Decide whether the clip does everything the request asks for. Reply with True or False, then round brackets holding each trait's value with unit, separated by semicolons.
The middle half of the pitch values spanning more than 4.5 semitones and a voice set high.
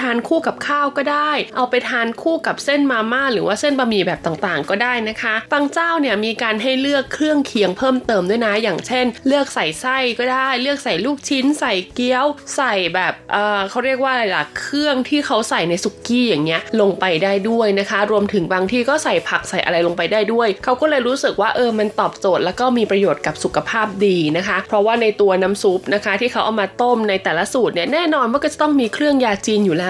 True (5.2 semitones; 230 Hz)